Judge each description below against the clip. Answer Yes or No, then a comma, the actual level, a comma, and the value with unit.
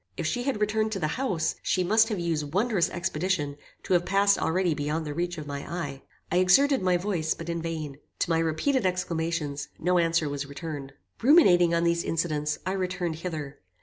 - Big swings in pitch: No, average, 3.2 semitones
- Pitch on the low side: No, medium, 170 Hz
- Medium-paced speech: Yes, average, 195 wpm